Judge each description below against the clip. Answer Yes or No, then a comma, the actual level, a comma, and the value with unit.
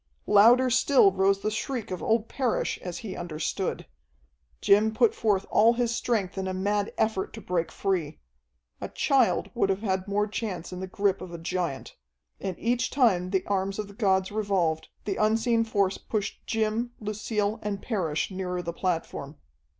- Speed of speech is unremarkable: Yes, average, 175 wpm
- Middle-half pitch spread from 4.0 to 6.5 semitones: No, average, 3.0 semitones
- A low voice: No, high, 200 Hz